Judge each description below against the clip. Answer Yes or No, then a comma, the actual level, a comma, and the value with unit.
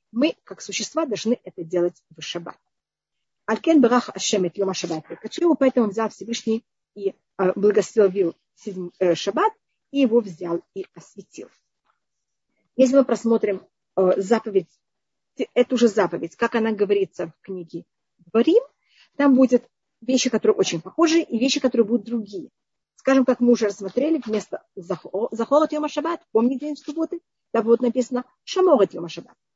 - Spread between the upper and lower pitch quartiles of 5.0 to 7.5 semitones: Yes, wide, 5.4 semitones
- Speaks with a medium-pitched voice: No, high, 230 Hz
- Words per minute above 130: Yes, average, 140 wpm